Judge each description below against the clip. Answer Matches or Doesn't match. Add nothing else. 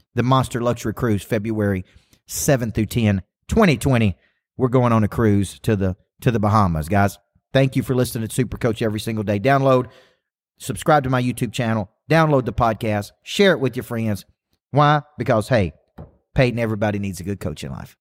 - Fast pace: Doesn't match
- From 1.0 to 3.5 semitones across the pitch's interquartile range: Doesn't match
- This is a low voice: Matches